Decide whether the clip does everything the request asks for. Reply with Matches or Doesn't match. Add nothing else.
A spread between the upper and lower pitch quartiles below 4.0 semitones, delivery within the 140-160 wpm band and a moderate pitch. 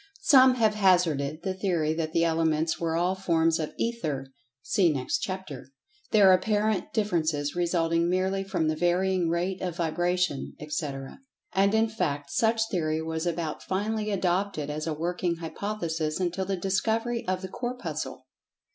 Matches